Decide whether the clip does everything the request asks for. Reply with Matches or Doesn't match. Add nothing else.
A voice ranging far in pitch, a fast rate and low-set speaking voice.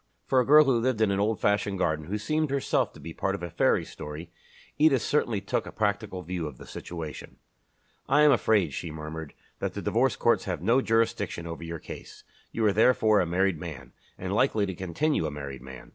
Matches